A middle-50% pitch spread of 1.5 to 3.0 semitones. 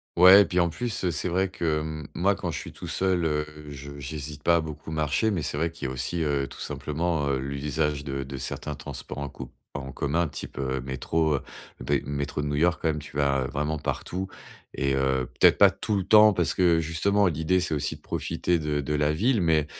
No: average, 3.4 semitones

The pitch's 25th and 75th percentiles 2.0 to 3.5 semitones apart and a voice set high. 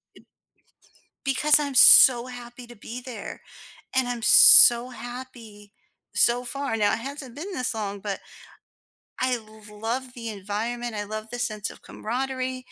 Yes: average, 2.8 semitones; high, 240 Hz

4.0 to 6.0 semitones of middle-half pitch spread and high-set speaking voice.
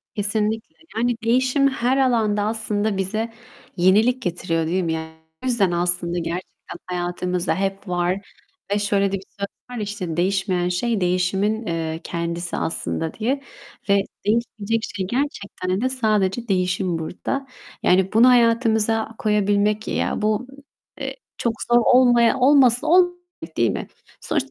Yes: average, 4.3 semitones; high, 205 Hz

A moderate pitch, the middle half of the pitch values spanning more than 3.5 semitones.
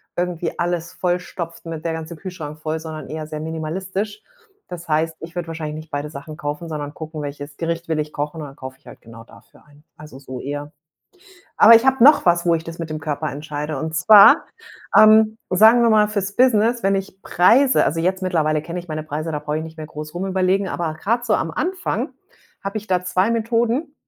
Yes: medium, 165 Hz; average, 4.1 semitones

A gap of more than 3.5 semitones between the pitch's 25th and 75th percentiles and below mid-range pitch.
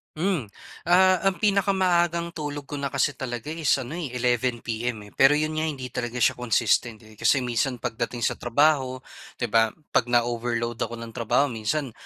Yes: average, 4.6 semitones; low, 125 Hz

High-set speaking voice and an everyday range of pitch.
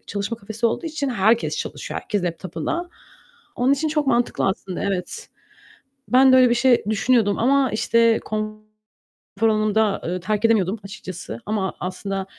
Yes: high, 220 Hz; average, 3.9 semitones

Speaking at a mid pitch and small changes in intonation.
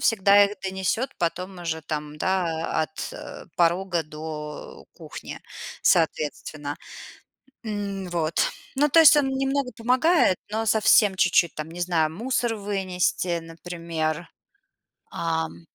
No: medium, 180 Hz; average, 4.6 semitones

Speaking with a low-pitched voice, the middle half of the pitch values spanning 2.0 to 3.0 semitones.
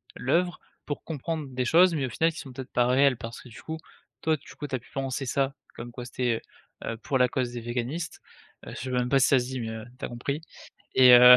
Yes: low, 130 Hz; narrow, 2.6 semitones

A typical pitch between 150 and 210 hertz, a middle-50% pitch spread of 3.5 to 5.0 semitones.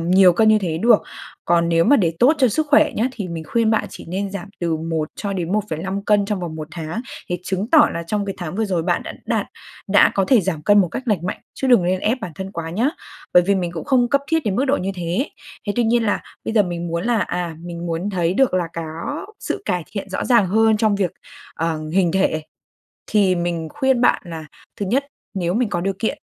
Yes: high, 190 Hz; average, 4.4 semitones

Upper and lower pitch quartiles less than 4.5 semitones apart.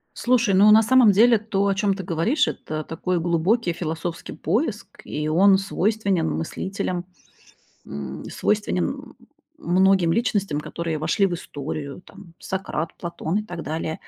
Yes: average, 4.1 semitones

